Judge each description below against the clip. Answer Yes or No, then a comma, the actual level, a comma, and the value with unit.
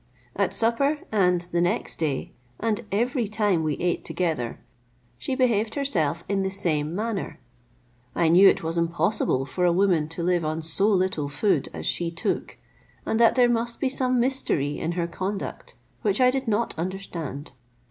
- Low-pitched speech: No, medium, 185 Hz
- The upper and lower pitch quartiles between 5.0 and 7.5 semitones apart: Yes, wide, 5.5 semitones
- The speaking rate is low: No, average, 170 wpm